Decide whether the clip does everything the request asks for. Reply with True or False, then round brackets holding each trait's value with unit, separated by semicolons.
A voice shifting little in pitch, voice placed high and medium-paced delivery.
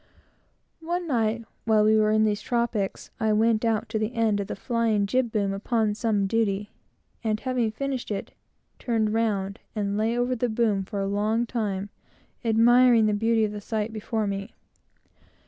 True (2.0 semitones; 220 Hz; 175 wpm)